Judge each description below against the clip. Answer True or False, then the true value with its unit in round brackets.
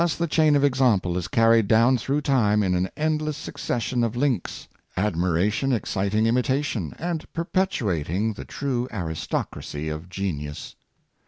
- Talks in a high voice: False (115 Hz)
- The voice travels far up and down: True (7.0 semitones)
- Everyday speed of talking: True (145 wpm)